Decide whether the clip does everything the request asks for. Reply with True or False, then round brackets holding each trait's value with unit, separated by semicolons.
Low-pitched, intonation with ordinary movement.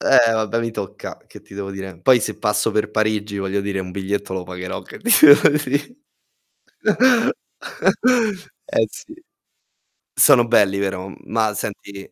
True (105 Hz; 3.1 semitones)